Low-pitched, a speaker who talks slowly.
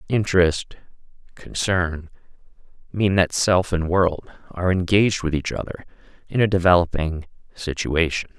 Yes: very low, 90 Hz; slow, 115 wpm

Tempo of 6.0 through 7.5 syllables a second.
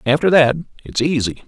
No: 5.7 syllables/s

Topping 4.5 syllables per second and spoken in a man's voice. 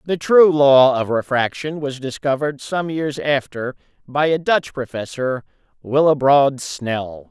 No: 4.1 syllables/s; male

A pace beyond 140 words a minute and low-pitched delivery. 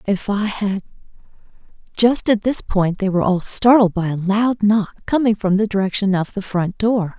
No: average, 190 wpm; high, 200 Hz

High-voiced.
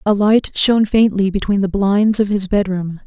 Yes: high, 200 Hz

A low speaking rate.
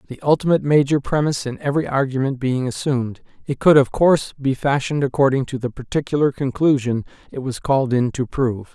No: average, 180 wpm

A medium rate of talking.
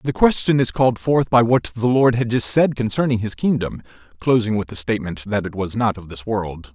No: fast, 230 wpm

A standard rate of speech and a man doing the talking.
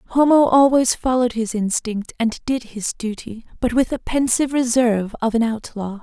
No: average, 170 wpm; female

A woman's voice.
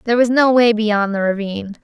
Yes: female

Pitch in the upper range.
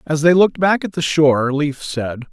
No: medium, 150 Hz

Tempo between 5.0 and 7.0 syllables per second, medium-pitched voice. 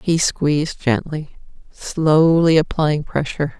No: 3.8 syllables/s; medium, 150 Hz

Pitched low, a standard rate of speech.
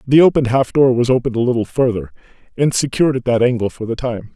No: low, 125 Hz; fast, 235 wpm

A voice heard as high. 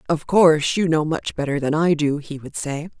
No: medium, 155 Hz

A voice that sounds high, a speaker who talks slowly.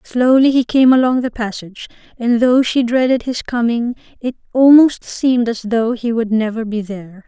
No: high, 240 Hz; average, 180 wpm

